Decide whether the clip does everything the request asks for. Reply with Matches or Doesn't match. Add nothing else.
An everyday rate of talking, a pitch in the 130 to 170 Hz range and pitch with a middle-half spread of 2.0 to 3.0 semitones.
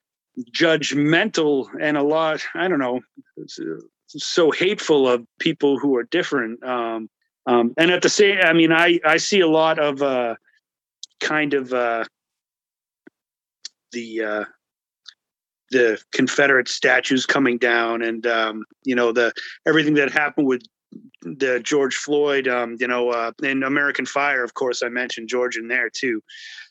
Doesn't match